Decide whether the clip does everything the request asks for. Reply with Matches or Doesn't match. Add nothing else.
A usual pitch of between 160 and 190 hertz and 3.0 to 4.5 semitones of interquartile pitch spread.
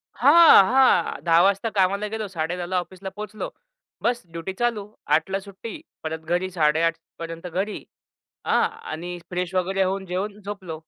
Matches